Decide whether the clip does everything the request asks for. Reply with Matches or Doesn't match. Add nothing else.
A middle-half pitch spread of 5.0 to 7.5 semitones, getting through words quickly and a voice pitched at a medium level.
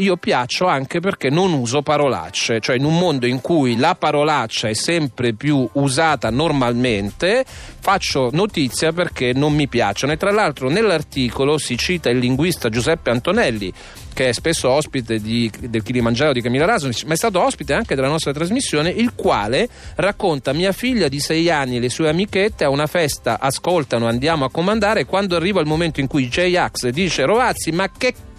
Matches